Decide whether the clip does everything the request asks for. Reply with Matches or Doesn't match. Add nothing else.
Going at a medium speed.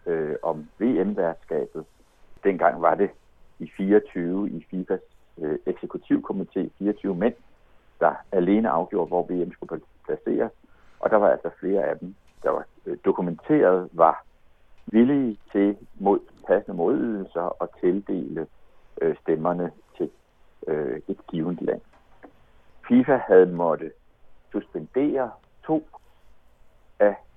Doesn't match